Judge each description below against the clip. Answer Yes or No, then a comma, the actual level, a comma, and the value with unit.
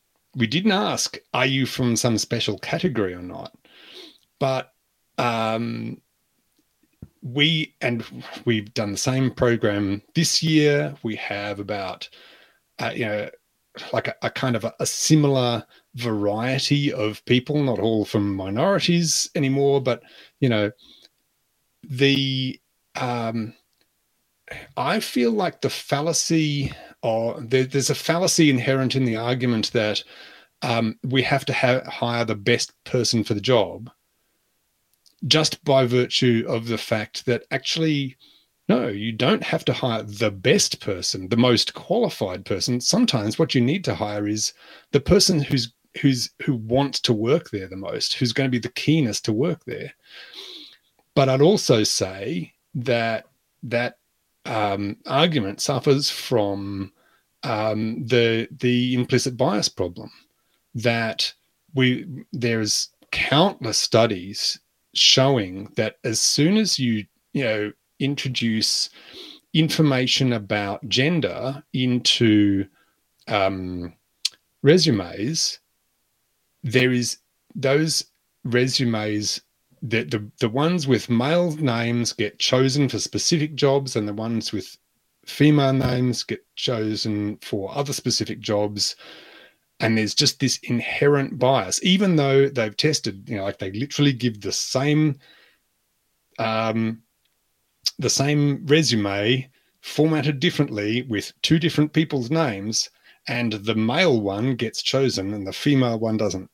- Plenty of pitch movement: No, average, 4.1 semitones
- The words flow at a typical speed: No, slow, 130 wpm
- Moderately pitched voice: No, low, 125 Hz